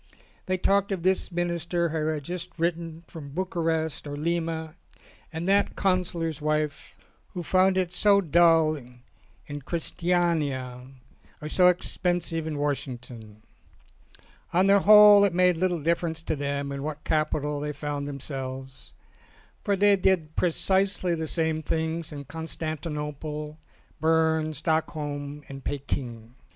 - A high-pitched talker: No, medium, 160 Hz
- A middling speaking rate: No, slow, 130 wpm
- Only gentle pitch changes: No, average, 3.2 semitones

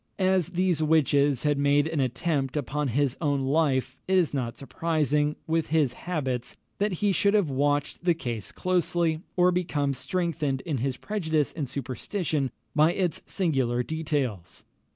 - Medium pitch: Yes, medium, 150 Hz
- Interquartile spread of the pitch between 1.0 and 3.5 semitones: No, average, 4.0 semitones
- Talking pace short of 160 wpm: Yes, average, 150 wpm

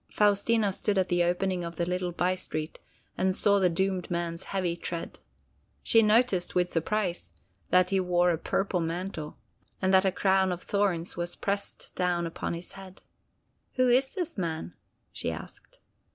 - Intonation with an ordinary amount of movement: No, narrow, 2.3 semitones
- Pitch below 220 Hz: Yes, medium, 185 Hz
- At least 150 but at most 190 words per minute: Yes, average, 165 wpm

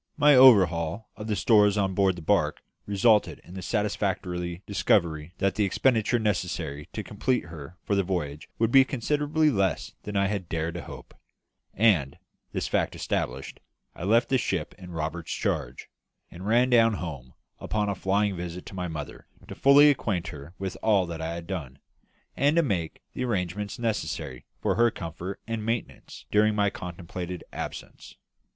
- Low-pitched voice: Yes, very low, 95 Hz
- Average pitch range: Yes, average, 4.3 semitones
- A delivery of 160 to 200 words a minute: Yes, average, 170 wpm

